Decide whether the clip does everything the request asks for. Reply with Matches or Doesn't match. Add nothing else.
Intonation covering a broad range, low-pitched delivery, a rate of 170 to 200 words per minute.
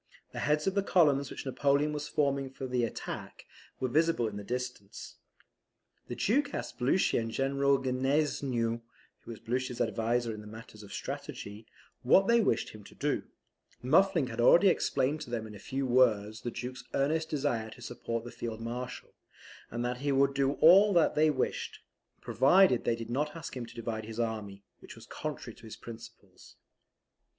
Doesn't match